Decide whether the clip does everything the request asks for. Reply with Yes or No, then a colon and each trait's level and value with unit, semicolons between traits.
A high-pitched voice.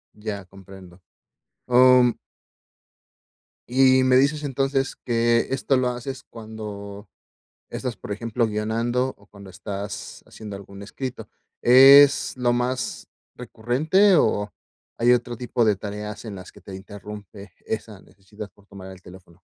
No: low, 110 Hz